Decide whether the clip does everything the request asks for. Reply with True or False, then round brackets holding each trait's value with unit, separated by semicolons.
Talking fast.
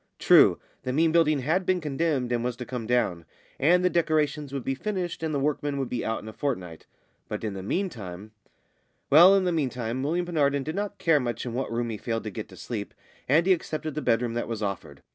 True (230 wpm)